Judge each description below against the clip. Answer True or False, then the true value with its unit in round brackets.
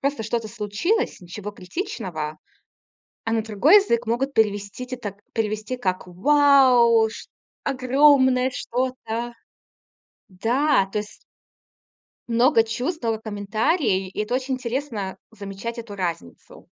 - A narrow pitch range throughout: False (4.0 semitones)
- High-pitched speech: True (230 Hz)